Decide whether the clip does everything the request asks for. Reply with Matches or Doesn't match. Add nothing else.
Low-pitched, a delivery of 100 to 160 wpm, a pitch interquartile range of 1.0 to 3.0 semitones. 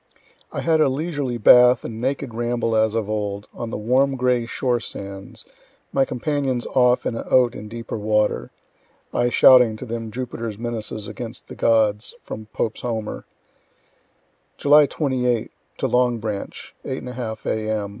Matches